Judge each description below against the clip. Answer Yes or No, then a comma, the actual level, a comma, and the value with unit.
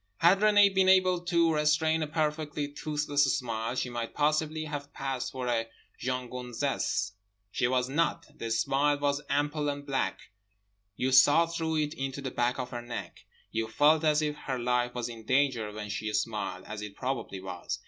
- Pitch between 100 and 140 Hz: Yes, low, 135 Hz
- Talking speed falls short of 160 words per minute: No, average, 180 wpm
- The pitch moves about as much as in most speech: Yes, average, 4.0 semitones